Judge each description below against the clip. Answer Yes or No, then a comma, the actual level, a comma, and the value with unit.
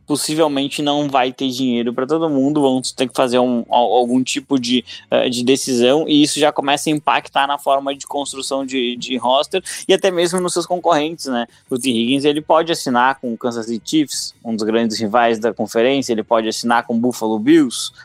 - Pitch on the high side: No, low, 135 Hz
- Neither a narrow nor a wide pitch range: Yes, average, 3.7 semitones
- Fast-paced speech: Yes, fast, 205 wpm